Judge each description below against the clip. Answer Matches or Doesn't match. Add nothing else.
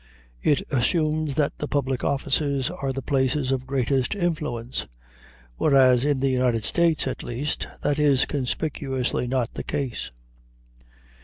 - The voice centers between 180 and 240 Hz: Doesn't match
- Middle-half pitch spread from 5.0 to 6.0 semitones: Doesn't match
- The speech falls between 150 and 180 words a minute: Doesn't match